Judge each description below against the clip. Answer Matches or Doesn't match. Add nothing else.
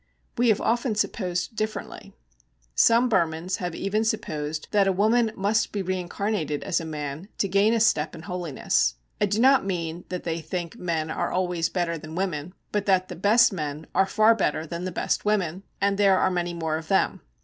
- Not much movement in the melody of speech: Doesn't match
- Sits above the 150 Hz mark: Matches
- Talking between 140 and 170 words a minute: Doesn't match